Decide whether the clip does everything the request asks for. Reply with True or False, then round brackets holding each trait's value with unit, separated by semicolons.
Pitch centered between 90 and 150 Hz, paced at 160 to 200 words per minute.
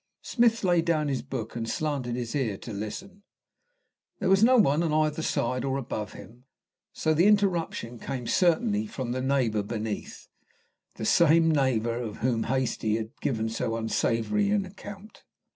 True (135 Hz; 165 wpm)